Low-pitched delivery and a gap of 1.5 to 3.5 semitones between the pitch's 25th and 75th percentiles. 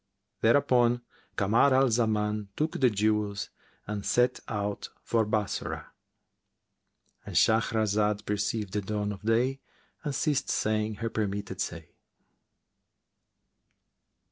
Yes: low, 110 Hz; narrow, 2.4 semitones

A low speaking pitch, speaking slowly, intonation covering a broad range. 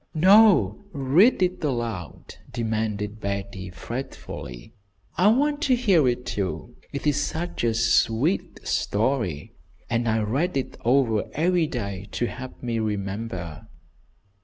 Yes: low, 120 Hz; slow, 125 wpm; wide, 6.8 semitones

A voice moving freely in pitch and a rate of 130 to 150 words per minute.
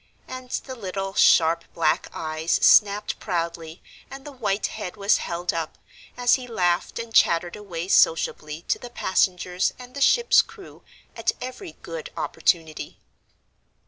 Yes: wide, 6.6 semitones; average, 145 wpm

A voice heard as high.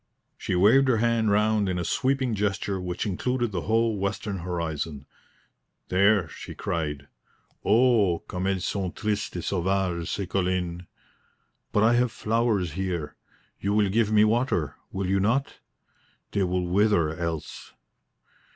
No: low, 100 Hz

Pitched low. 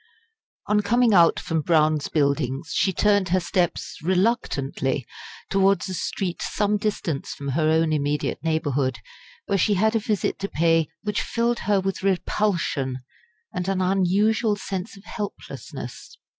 No: medium, 185 Hz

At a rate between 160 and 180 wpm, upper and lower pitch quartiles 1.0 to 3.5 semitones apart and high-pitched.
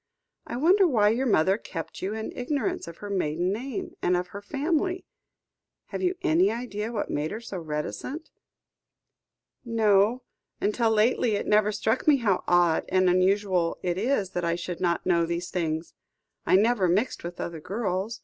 No: average, 170 wpm; average, 5.0 semitones; high, 205 Hz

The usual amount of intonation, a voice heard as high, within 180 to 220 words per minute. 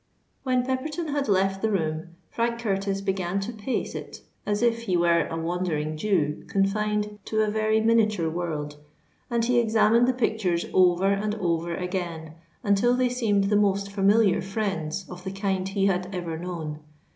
No: average, 3.8 semitones; high, 195 Hz; average, 170 wpm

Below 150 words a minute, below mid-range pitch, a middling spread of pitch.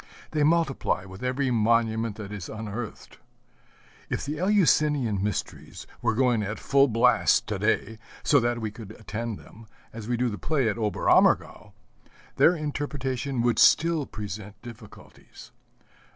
Yes: average, 140 wpm; low, 115 Hz; average, 4.4 semitones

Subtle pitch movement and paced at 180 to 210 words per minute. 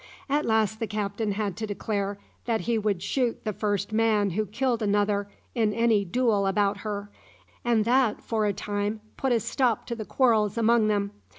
Yes: narrow, 2.1 semitones; average, 185 wpm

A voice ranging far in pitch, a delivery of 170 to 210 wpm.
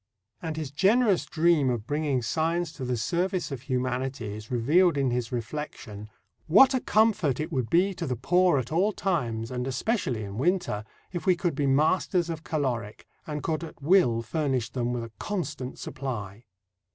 Yes: wide, 5.9 semitones; average, 175 wpm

